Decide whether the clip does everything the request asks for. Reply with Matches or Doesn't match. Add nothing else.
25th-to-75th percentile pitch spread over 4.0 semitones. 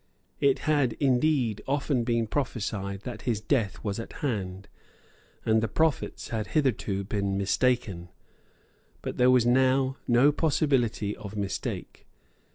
Matches